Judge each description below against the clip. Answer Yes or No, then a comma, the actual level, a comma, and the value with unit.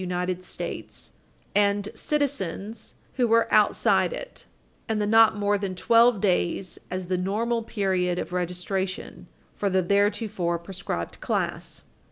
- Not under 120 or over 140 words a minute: Yes, slow, 135 wpm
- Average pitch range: Yes, average, 3.2 semitones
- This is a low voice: No, high, 200 Hz